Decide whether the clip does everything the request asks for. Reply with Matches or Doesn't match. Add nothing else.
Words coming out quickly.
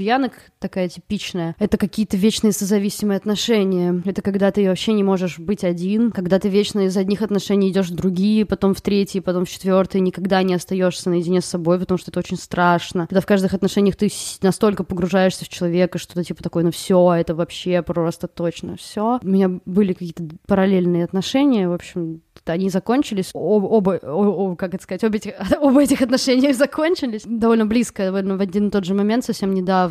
Matches